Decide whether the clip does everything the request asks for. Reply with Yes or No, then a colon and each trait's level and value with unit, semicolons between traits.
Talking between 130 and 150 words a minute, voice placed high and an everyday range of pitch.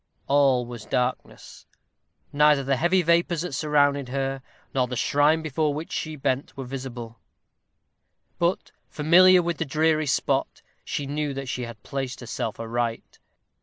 No: average, 145 wpm; medium, 140 Hz; average, 3.5 semitones